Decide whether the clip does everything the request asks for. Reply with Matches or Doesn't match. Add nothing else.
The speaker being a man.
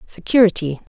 Doesn't match